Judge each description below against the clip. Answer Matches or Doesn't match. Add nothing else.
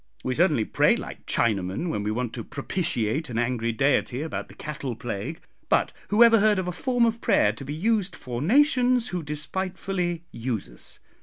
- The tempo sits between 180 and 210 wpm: Matches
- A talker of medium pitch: Matches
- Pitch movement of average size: Doesn't match